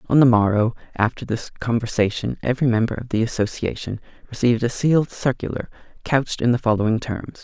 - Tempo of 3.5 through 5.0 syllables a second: No, 6.1 syllables/s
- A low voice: Yes, low, 120 Hz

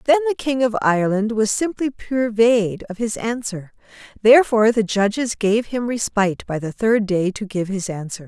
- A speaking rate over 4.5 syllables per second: Yes, 5.0 syllables/s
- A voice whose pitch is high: Yes, high, 220 Hz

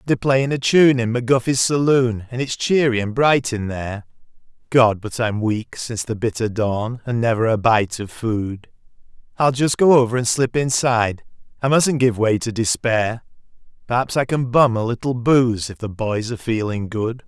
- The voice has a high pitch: No, low, 120 Hz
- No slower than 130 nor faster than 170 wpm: No, average, 180 wpm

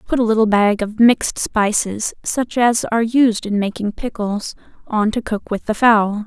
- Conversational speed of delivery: Yes, average, 190 wpm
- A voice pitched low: No, high, 220 Hz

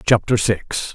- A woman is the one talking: No, male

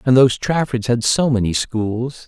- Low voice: Yes, low, 120 Hz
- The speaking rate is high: No, average, 185 wpm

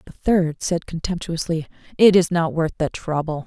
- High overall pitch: No, medium, 165 Hz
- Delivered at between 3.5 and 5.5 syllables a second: Yes, 5.0 syllables/s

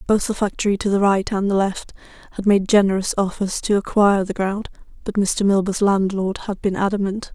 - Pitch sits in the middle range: No, high, 200 Hz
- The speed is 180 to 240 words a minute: Yes, average, 195 wpm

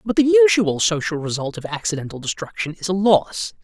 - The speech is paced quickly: No, average, 180 wpm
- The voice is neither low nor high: Yes, medium, 180 Hz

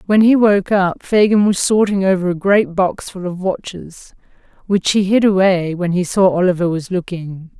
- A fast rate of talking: No, average, 190 wpm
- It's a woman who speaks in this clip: Yes, female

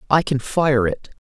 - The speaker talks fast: No, average, 195 wpm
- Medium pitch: Yes, medium, 155 Hz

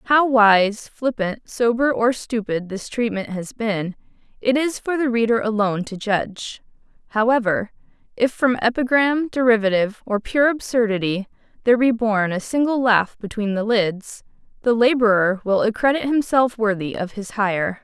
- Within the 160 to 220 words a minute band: No, average, 150 wpm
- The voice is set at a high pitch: Yes, high, 225 Hz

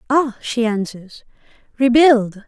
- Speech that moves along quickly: No, slow, 95 wpm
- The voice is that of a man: No, female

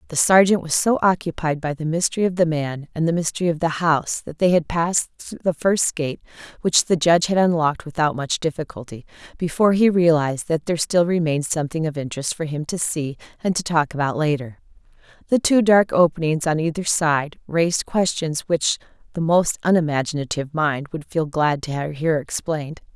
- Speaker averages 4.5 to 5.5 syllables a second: Yes, 5.0 syllables/s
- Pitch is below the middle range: No, medium, 160 Hz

